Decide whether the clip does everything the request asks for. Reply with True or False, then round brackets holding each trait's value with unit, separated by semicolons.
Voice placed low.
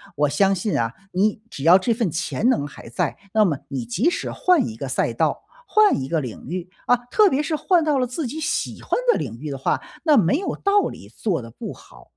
False (195 Hz)